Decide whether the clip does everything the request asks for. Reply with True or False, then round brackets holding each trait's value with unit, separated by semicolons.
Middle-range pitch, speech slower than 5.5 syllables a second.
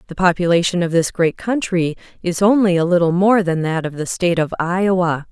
False (175 Hz; 5.6 syllables/s)